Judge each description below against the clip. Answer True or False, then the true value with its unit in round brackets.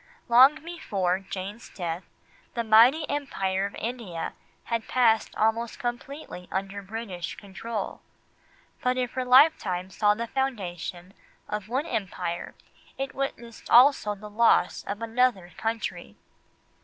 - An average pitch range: True (4.5 semitones)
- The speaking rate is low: True (120 wpm)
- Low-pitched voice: False (225 Hz)